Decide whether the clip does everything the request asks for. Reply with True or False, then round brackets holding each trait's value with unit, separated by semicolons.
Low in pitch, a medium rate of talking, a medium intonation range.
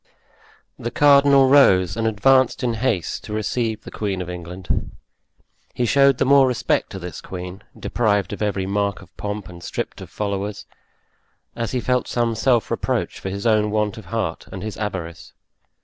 True (105 Hz; 175 wpm; 4.1 semitones)